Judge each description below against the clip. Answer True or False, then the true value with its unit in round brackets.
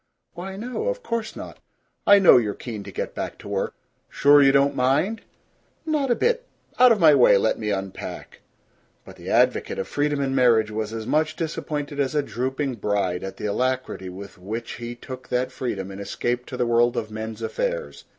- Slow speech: False (200 wpm)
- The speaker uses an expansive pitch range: True (6.0 semitones)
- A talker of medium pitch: False (130 Hz)